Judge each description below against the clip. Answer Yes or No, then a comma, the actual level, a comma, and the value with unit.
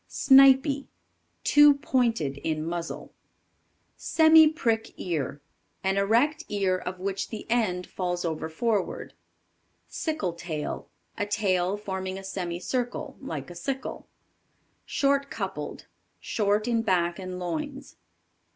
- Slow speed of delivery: Yes, slow, 115 wpm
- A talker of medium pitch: No, high, 195 Hz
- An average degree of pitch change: No, wide, 6.3 semitones